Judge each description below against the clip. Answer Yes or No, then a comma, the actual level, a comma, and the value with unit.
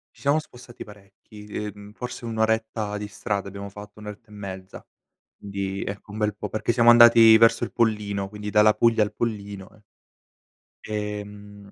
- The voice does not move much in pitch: Yes, narrow, 1.7 semitones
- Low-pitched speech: Yes, low, 105 Hz